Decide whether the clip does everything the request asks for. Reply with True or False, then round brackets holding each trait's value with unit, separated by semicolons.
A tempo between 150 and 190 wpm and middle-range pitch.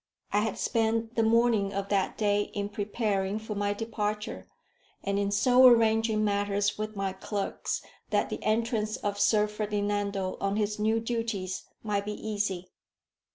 False (155 wpm; 210 Hz)